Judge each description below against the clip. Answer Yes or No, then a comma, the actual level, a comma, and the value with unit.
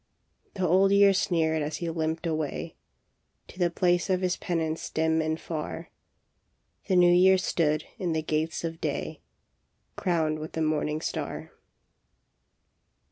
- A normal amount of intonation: No, narrow, 2.3 semitones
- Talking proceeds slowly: No, average, 145 wpm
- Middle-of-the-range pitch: Yes, medium, 165 Hz